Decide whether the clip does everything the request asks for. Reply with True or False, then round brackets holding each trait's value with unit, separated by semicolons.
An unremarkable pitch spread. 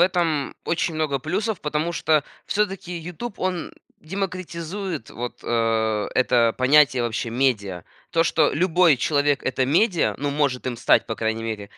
False (6.2 semitones)